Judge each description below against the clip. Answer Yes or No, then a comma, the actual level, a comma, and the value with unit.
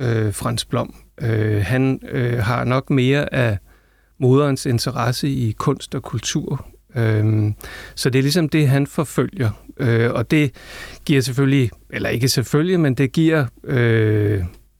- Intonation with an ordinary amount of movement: Yes, average, 3.6 semitones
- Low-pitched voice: Yes, low, 130 Hz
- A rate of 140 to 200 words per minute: Yes, slow, 145 wpm